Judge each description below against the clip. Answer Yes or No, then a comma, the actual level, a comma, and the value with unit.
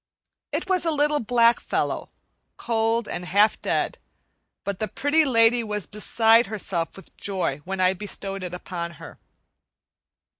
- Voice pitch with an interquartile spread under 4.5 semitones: Yes, average, 3.7 semitones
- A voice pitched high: Yes, high, 210 Hz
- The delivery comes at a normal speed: Yes, average, 145 wpm